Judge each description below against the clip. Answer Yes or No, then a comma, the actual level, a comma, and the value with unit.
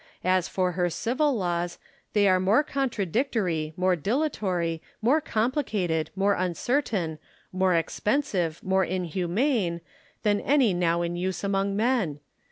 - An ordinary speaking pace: No, slow, 130 wpm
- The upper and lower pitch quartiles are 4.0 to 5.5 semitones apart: Yes, average, 4.7 semitones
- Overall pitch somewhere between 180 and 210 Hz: Yes, high, 190 Hz